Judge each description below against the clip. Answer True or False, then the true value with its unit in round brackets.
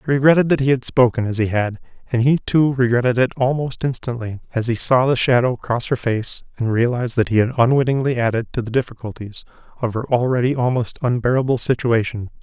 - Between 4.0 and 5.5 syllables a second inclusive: False (6.0 syllables/s)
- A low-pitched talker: True (125 Hz)